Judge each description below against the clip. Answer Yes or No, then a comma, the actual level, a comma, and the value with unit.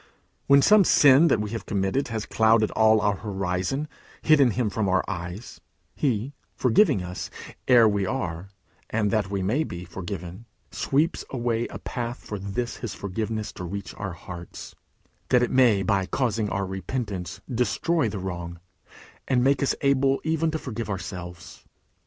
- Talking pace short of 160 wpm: No, average, 165 wpm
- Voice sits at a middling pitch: No, low, 110 Hz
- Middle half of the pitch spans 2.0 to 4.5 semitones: No, average, 5.1 semitones